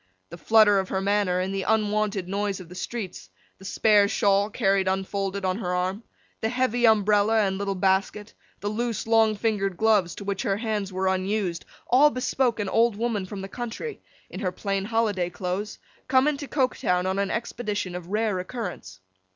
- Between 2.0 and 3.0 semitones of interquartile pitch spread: Yes, average, 2.7 semitones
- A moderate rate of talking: Yes, average, 185 wpm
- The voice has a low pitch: No, high, 200 Hz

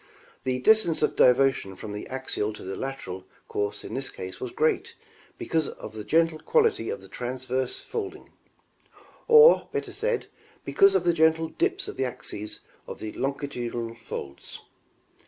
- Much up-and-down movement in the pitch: Yes, wide, 6.5 semitones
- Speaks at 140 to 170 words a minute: Yes, average, 160 wpm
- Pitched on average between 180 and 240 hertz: No, low, 135 Hz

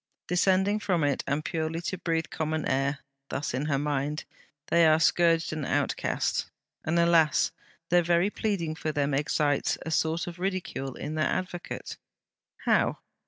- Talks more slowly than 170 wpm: Yes, average, 155 wpm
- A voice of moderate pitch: Yes, medium, 160 Hz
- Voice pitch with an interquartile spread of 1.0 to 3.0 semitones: Yes, average, 2.7 semitones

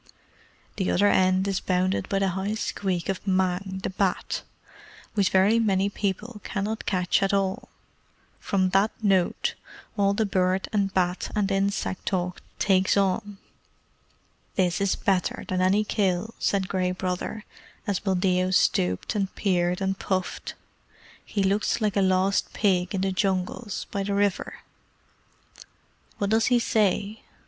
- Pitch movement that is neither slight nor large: No, narrow, 1.5 semitones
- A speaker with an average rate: Yes, average, 145 wpm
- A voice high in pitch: Yes, high, 195 Hz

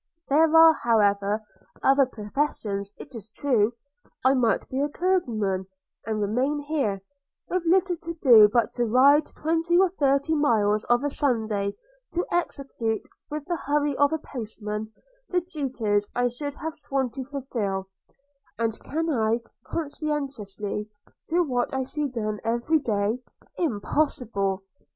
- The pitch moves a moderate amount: No, wide, 5.7 semitones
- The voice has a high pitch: Yes, very high, 260 Hz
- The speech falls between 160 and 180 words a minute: No, average, 145 wpm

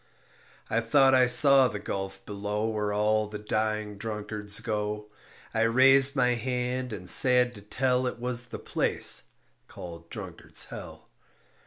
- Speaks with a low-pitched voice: Yes, low, 110 Hz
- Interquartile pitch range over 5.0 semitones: No, average, 3.2 semitones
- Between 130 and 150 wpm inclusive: Yes, average, 145 wpm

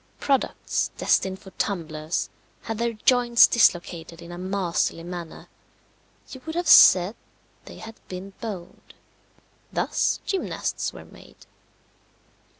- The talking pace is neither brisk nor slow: No, slow, 115 wpm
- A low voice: No, high, 190 Hz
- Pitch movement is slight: No, average, 5.2 semitones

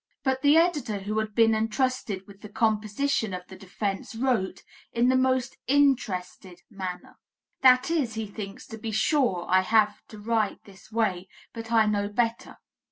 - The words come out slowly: No, average, 165 wpm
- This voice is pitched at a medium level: No, high, 220 Hz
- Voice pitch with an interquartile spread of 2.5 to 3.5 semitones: No, average, 4.1 semitones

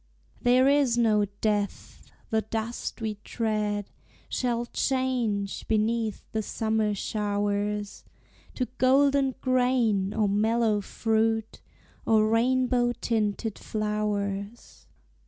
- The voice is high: Yes, high, 220 Hz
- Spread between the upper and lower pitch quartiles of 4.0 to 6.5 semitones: No, narrow, 2.5 semitones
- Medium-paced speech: No, slow, 95 wpm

